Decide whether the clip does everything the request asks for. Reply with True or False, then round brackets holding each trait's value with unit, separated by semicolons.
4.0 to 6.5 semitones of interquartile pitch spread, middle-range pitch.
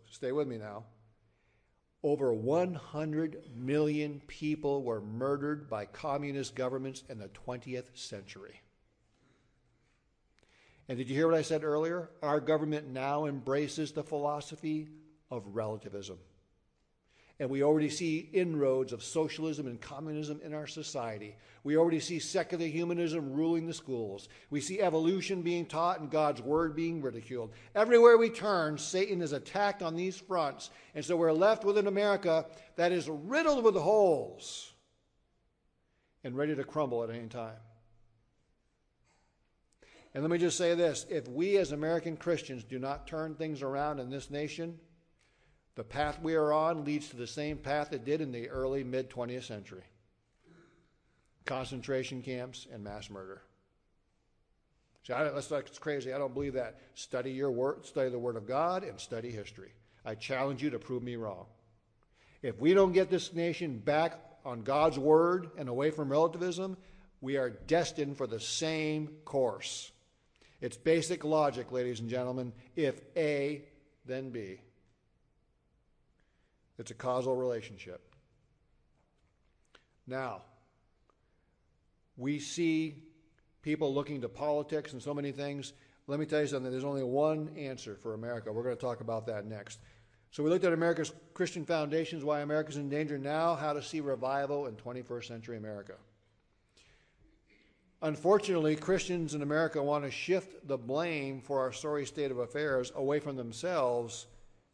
True (4.5 semitones; 145 Hz)